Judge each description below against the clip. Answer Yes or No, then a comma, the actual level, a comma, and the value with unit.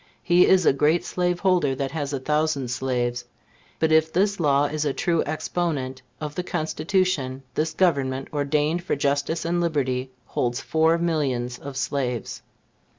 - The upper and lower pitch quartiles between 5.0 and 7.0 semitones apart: No, average, 4.0 semitones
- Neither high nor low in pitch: Yes, medium, 150 Hz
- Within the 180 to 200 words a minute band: No, average, 155 wpm